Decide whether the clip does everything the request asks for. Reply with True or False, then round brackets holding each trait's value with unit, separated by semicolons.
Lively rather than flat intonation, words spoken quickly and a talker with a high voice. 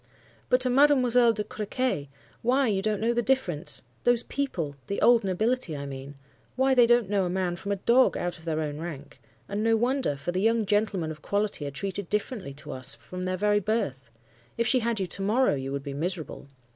True (7.0 semitones; 210 wpm; 200 Hz)